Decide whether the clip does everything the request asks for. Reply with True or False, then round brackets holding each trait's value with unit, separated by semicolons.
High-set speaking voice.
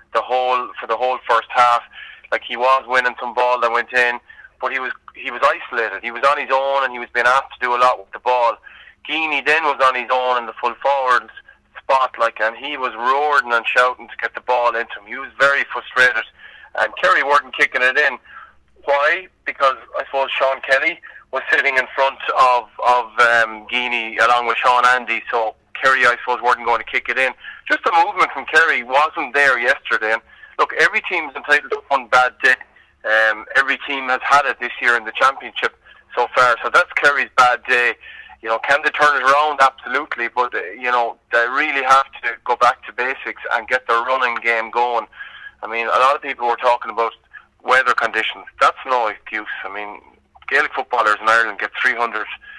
False (125 Hz)